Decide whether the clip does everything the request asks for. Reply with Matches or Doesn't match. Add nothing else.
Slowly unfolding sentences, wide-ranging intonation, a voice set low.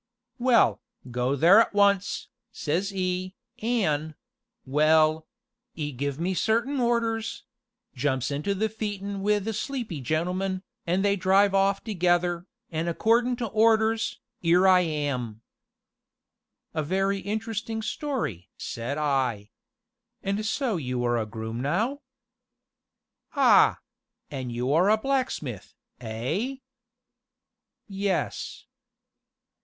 Doesn't match